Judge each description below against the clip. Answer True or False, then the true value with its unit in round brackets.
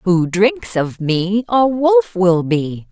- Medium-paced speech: True (165 wpm)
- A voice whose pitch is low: False (205 Hz)